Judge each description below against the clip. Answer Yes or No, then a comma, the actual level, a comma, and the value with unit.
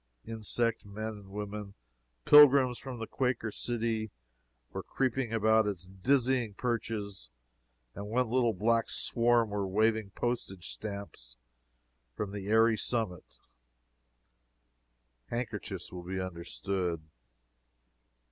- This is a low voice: Yes, low, 110 Hz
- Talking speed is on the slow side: Yes, slow, 105 wpm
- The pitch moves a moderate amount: Yes, average, 3.0 semitones